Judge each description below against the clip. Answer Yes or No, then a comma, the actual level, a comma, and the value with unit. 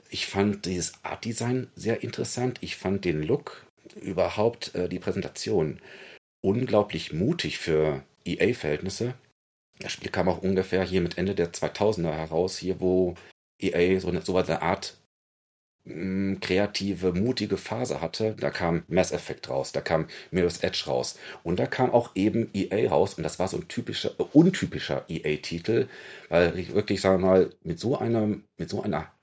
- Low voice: Yes, very low, 95 Hz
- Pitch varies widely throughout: No, average, 2.9 semitones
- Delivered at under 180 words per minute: Yes, average, 165 wpm